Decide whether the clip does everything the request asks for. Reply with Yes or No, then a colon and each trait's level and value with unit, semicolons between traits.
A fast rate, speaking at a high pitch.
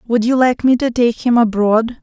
Yes: fast, 235 wpm; high, 235 Hz